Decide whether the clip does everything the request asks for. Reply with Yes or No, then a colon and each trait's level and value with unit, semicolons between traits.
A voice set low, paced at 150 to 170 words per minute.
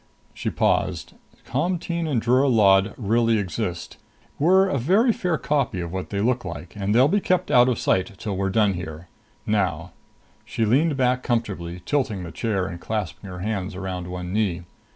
No: low, 105 Hz; average, 180 wpm